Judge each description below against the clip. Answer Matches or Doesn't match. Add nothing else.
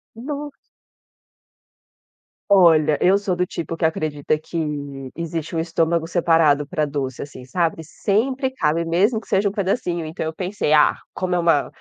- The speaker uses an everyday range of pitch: Matches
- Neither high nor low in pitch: Matches